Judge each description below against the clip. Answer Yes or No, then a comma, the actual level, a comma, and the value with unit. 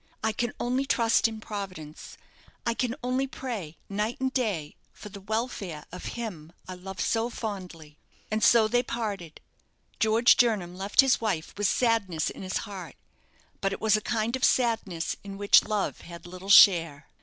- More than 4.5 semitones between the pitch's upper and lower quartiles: No, average, 4.2 semitones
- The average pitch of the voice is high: Yes, high, 210 Hz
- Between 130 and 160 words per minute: No, average, 170 wpm